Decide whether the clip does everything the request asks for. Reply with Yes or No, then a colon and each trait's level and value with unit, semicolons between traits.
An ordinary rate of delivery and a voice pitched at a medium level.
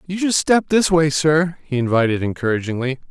Yes: average, 175 wpm; medium, 145 Hz